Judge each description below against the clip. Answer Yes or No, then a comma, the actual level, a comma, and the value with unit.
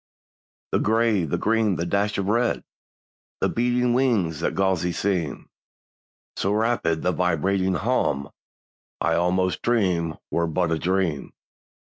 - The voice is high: No, very low, 95 Hz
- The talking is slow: Yes, slow, 130 wpm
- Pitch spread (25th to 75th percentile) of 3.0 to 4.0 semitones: No, average, 4.7 semitones